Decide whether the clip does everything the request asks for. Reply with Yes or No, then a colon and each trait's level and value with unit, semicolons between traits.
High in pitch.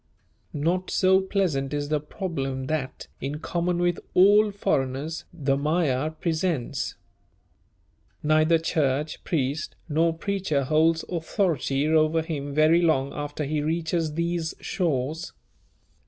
No: medium, 155 Hz